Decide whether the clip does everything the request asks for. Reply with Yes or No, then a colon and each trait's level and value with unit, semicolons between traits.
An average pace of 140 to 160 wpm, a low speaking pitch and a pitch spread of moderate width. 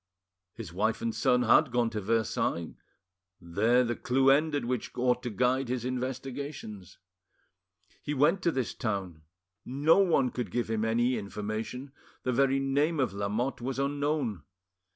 Yes: average, 150 wpm; low, 125 Hz; average, 3.5 semitones